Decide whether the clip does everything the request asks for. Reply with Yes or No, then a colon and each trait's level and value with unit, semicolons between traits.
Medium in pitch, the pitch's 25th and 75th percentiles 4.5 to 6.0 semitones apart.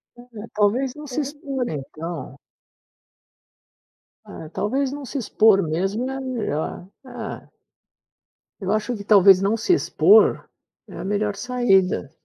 No: high, 215 Hz; average, 5.1 semitones